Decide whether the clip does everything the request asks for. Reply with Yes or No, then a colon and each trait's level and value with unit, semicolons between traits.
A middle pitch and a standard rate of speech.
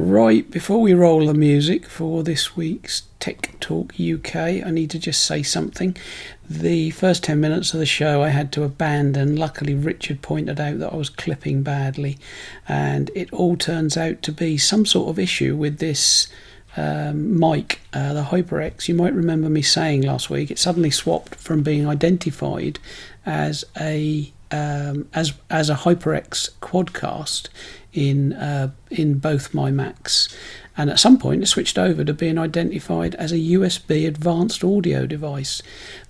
Yes: medium, 150 Hz; average, 165 wpm